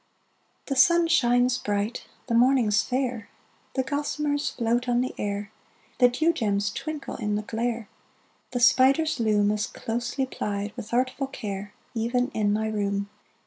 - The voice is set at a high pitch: Yes, high, 240 Hz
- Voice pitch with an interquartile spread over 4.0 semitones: No, average, 3.7 semitones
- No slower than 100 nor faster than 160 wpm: Yes, average, 145 wpm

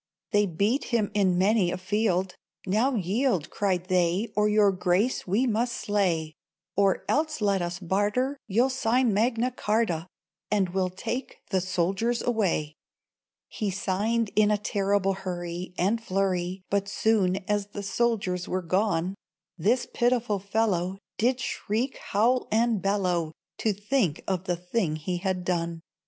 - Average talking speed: Yes, average, 145 wpm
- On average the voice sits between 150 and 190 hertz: No, high, 200 Hz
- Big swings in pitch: No, average, 3.5 semitones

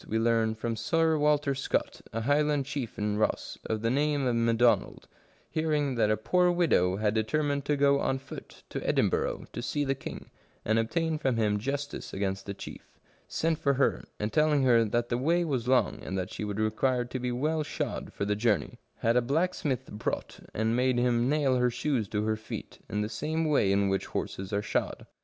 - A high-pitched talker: No, low, 125 Hz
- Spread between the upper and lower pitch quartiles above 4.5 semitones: Yes, average, 4.9 semitones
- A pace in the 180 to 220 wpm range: Yes, fast, 205 wpm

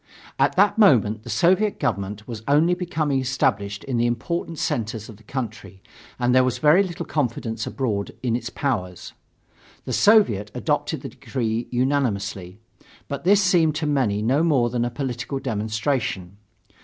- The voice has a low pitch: Yes, low, 125 Hz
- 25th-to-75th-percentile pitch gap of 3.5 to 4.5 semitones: No, wide, 5.5 semitones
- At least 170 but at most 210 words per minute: No, average, 155 wpm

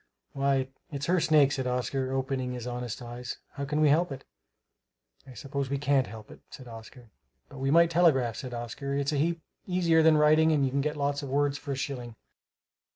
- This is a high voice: No, medium, 140 Hz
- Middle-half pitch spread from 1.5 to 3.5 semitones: Yes, average, 2.9 semitones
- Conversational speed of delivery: No, fast, 210 wpm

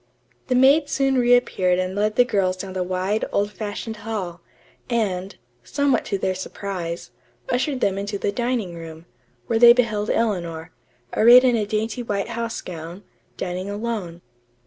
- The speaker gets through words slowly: No, average, 155 wpm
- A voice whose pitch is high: Yes, high, 205 Hz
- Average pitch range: Yes, average, 4.3 semitones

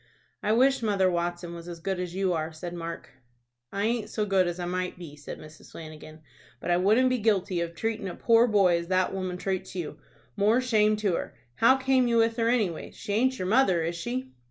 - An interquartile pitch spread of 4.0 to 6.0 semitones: Yes, average, 4.5 semitones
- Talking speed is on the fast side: Yes, fast, 230 wpm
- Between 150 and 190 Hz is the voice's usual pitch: Yes, medium, 185 Hz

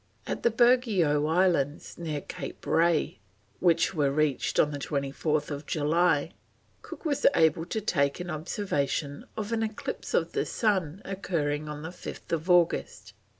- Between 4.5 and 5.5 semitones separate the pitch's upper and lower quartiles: No, average, 4.1 semitones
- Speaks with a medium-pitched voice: Yes, medium, 165 Hz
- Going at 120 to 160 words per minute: Yes, slow, 135 wpm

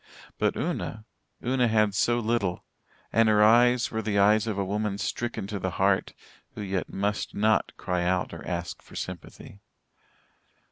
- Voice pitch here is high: No, low, 105 Hz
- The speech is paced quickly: No, average, 160 wpm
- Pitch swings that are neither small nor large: No, narrow, 2.3 semitones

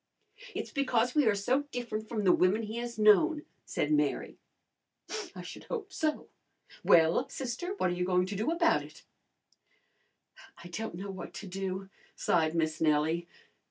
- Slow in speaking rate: No, average, 160 wpm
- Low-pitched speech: No, high, 210 Hz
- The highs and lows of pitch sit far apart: Yes, wide, 6.4 semitones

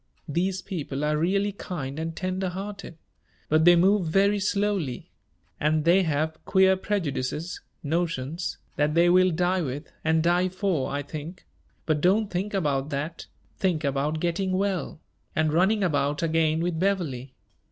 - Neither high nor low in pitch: Yes, medium, 170 Hz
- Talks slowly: No, average, 150 wpm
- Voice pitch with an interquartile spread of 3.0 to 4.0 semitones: Yes, average, 3.7 semitones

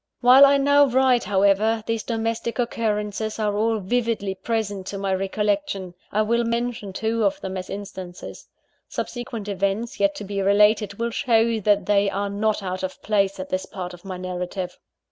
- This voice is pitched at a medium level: No, high, 210 Hz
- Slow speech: No, average, 175 wpm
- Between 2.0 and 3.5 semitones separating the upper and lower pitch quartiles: Yes, average, 2.8 semitones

